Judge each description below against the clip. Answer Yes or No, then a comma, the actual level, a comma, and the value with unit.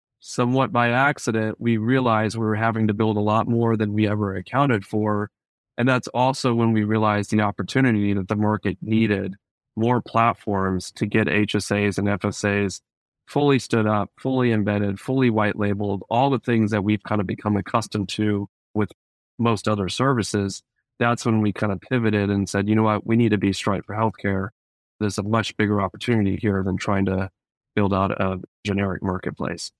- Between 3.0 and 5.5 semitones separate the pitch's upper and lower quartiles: No, narrow, 2.4 semitones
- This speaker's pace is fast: No, average, 185 wpm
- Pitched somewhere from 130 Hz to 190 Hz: No, low, 105 Hz